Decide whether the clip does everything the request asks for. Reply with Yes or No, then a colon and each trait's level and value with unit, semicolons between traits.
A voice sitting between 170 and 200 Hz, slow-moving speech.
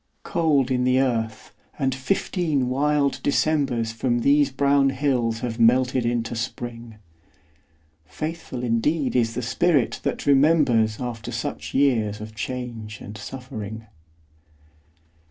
No: low, 125 Hz; slow, 120 wpm